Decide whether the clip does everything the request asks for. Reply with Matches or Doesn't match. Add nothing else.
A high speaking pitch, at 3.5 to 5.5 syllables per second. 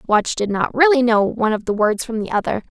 Doesn't match